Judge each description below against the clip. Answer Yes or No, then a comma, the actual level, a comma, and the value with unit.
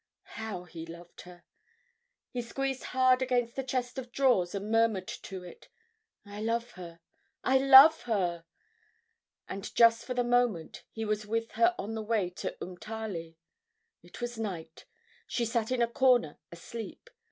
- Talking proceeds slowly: No, average, 155 wpm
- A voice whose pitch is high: Yes, high, 225 Hz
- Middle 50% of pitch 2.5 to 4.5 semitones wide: No, average, 5.1 semitones